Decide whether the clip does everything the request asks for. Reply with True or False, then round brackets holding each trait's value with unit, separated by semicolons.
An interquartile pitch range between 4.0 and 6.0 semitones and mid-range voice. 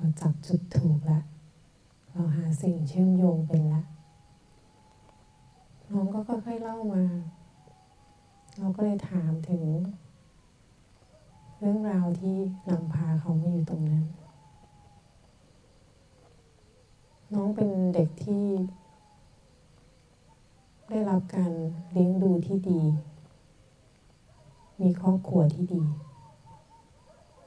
False (3.6 semitones; 165 Hz)